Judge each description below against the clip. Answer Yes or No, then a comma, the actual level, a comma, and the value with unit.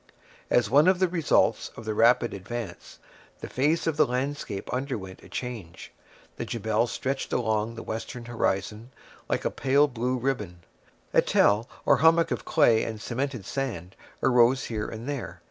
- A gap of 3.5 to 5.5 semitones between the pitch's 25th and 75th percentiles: Yes, average, 4.0 semitones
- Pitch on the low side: Yes, low, 120 Hz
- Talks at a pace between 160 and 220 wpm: Yes, average, 165 wpm